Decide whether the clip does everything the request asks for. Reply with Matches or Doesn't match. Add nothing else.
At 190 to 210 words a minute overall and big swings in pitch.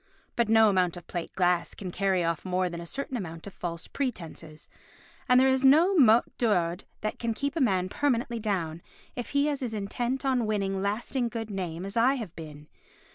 Matches